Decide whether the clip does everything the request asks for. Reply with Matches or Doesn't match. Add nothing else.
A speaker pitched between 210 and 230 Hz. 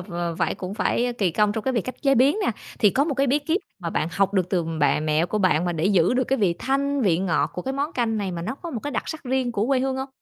Matches